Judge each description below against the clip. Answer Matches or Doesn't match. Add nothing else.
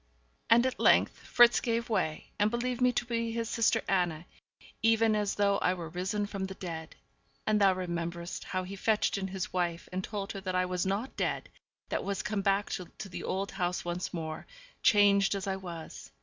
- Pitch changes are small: Doesn't match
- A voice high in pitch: Matches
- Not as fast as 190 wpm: Doesn't match